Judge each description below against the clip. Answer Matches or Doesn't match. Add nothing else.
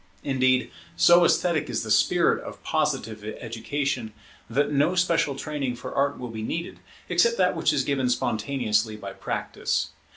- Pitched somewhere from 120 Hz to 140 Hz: Matches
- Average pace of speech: Matches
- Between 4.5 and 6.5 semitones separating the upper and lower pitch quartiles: Matches